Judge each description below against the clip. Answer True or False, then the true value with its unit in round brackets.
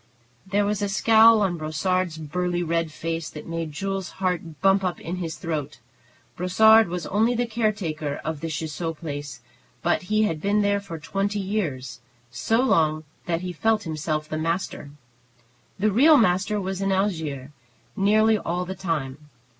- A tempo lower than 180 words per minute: True (160 wpm)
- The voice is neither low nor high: True (180 Hz)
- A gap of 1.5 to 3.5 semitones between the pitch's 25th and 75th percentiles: False (4.3 semitones)